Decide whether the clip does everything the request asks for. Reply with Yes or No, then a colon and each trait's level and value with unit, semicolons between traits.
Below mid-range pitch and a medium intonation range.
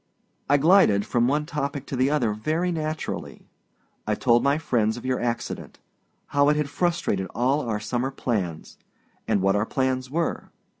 Yes: low, 130 Hz; average, 4.4 semitones